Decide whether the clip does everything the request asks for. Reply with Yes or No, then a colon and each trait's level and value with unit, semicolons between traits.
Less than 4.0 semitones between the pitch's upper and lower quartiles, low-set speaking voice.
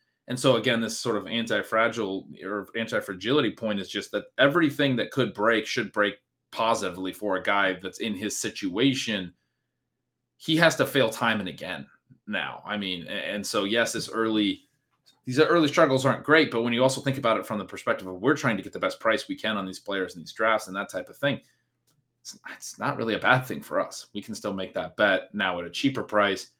No: average, 4.5 semitones; low, 115 Hz